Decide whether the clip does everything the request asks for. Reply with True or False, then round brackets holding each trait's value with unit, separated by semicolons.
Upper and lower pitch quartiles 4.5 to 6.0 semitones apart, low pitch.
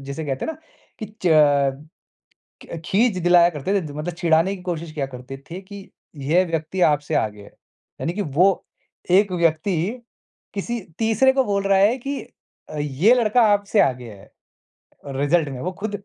False (5.4 semitones; 175 Hz)